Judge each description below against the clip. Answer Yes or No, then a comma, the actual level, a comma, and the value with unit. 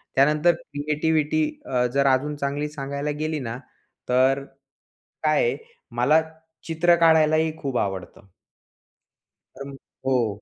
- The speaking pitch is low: No, medium, 145 Hz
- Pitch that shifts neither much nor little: Yes, average, 3.0 semitones